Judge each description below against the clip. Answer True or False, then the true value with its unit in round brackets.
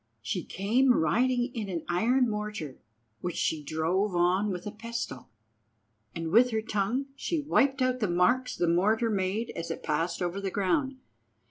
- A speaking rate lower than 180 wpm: True (165 wpm)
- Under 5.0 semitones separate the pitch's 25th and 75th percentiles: False (5.6 semitones)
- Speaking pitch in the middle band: False (205 Hz)